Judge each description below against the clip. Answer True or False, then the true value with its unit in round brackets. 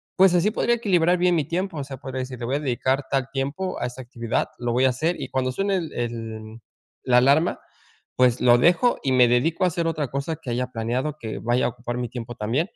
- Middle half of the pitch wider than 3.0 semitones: True (5.3 semitones)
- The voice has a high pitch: False (130 Hz)